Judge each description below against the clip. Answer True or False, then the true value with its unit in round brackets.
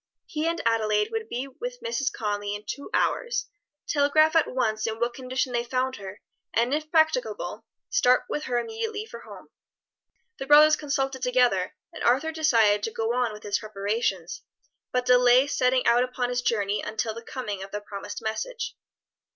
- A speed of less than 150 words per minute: False (175 wpm)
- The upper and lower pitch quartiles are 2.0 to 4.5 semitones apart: False (5.5 semitones)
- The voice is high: True (250 Hz)